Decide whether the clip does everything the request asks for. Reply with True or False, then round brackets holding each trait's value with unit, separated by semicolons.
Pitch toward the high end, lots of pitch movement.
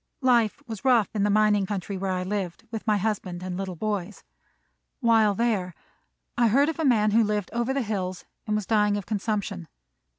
False (210 Hz; 2.8 semitones)